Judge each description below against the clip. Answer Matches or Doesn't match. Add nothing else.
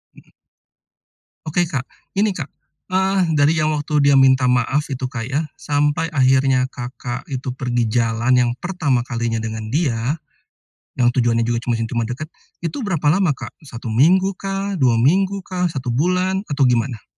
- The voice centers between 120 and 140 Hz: Matches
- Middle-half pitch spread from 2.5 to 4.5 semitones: Doesn't match